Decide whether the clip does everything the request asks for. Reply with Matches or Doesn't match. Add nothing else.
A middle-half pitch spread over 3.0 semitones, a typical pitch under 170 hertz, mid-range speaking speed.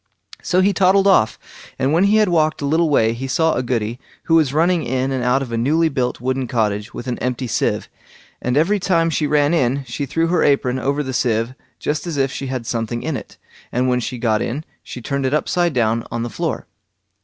Doesn't match